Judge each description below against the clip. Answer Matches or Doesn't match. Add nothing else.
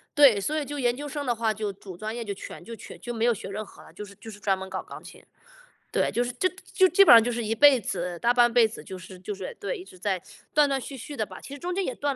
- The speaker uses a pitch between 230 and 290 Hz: Matches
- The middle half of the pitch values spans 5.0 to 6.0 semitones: Matches